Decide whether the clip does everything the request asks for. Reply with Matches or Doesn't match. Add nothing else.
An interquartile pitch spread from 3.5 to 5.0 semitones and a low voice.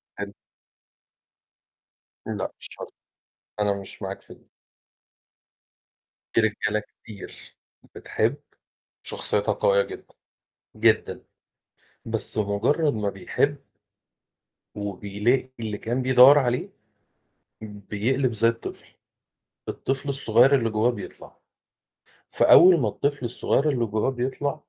Matches